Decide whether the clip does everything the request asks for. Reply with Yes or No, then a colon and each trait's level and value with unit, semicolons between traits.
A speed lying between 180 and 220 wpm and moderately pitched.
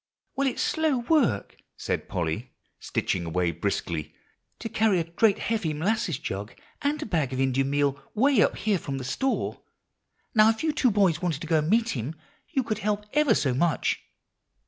Yes: average, 185 wpm; medium, 175 Hz